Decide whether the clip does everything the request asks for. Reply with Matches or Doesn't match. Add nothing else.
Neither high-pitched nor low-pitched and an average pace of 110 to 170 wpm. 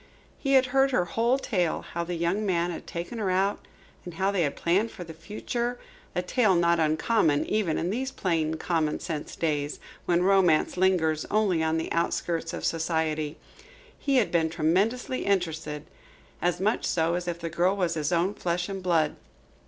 Doesn't match